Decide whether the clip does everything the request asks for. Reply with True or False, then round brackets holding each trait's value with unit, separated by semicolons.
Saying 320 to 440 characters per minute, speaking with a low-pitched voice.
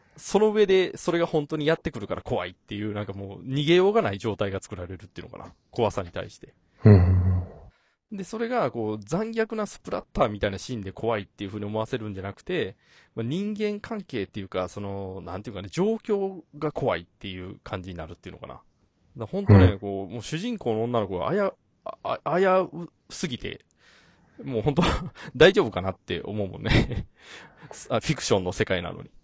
True (385 characters per minute; 110 Hz)